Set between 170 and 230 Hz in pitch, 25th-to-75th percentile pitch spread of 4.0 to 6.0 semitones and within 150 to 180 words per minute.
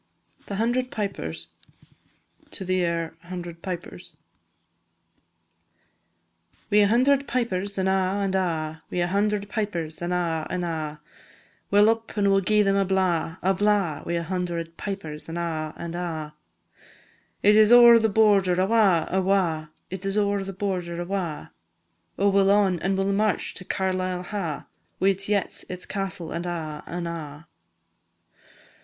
No: medium, 185 Hz; average, 3.0 semitones; average, 160 wpm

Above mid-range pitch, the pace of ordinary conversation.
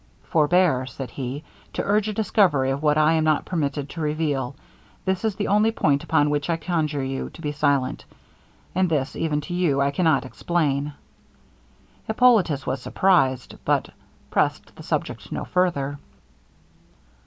No: medium, 150 Hz; average, 155 wpm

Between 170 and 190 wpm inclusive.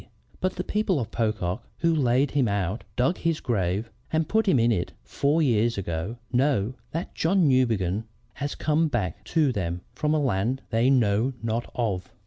Yes: average, 175 wpm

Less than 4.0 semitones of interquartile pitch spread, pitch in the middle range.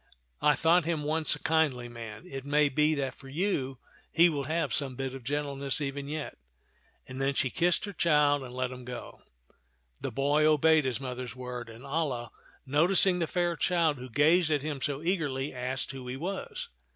Yes: average, 3.5 semitones; medium, 145 Hz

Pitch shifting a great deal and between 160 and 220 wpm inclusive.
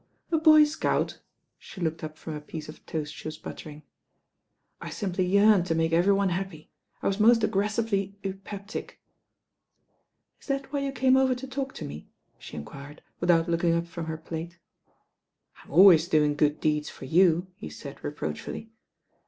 No: average, 5.0 semitones; average, 175 wpm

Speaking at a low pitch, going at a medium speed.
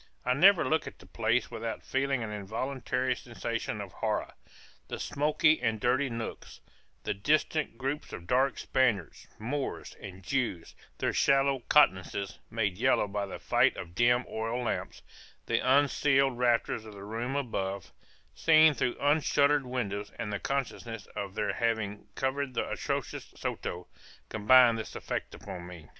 Yes: low, 120 Hz; average, 150 wpm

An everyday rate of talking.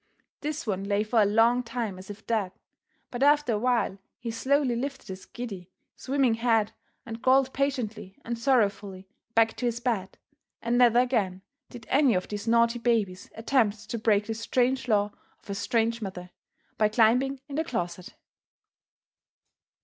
Yes: average, 165 wpm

